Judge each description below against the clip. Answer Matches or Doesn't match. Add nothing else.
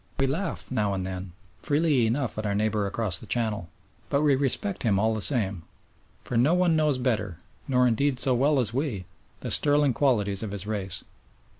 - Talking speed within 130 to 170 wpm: Doesn't match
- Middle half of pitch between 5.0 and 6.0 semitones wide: Matches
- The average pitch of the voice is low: Matches